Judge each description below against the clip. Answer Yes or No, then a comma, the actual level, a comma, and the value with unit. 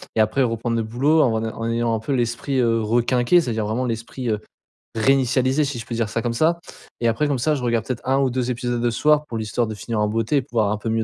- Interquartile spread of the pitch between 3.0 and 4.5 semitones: No, narrow, 2.6 semitones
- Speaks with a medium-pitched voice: No, low, 120 Hz